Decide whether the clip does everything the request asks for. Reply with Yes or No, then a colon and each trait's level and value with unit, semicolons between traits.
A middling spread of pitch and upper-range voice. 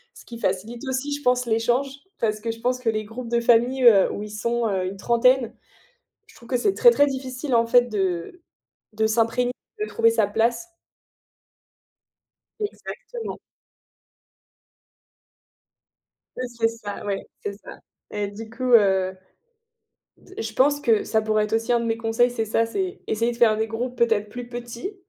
No: narrow, 2.3 semitones; high, 230 Hz